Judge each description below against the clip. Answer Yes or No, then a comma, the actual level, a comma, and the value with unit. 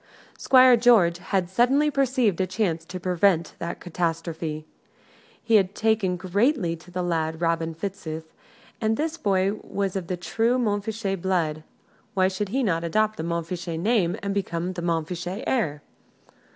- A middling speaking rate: Yes, average, 150 wpm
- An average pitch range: Yes, average, 4.3 semitones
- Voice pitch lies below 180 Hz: No, medium, 185 Hz